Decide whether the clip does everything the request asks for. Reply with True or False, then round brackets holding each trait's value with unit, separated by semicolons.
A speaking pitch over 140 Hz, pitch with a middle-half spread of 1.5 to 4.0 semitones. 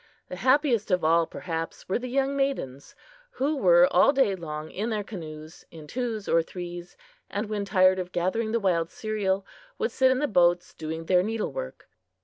False (190 Hz; 5.3 semitones)